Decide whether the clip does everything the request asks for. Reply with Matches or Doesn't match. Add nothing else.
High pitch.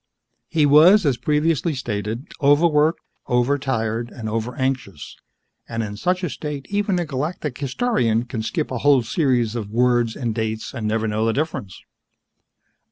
Doesn't match